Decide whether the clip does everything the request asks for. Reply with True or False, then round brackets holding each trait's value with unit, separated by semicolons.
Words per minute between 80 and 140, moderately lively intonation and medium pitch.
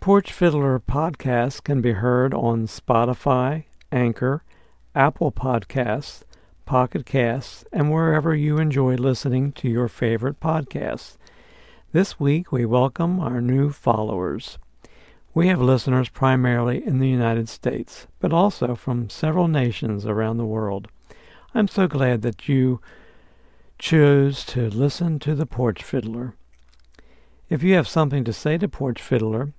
False (135 wpm; 4.2 semitones; 130 Hz)